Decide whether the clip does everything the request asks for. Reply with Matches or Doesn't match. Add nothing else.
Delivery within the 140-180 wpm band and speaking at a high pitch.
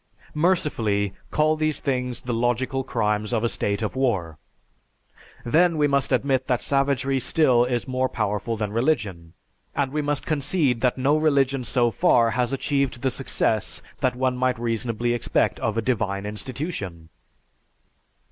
Doesn't match